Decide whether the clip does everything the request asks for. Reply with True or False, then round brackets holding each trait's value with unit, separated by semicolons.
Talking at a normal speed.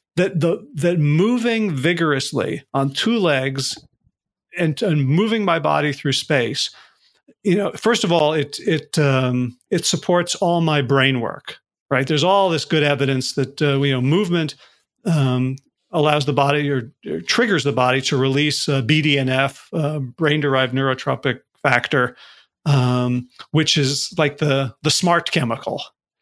True (155 wpm)